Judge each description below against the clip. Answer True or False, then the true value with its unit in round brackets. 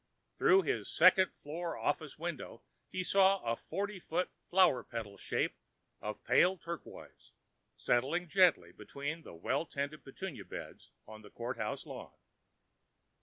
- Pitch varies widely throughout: True (7.0 semitones)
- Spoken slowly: True (130 wpm)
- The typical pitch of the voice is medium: True (160 Hz)